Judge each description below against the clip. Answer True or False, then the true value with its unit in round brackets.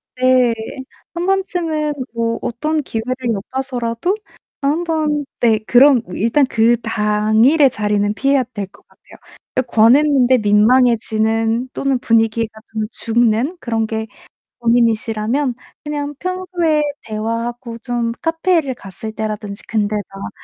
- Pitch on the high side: True (240 Hz)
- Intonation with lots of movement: False (4.5 semitones)